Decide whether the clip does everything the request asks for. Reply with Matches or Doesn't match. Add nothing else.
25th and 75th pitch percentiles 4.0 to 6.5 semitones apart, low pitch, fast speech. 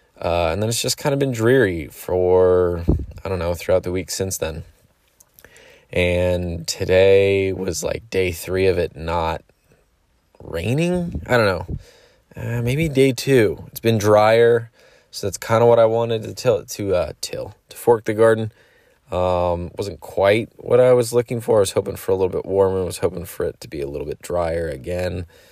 Doesn't match